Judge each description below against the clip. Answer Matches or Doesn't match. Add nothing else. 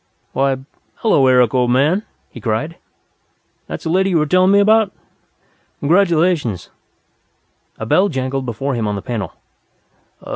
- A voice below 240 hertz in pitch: Matches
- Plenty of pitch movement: Matches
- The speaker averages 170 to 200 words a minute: Doesn't match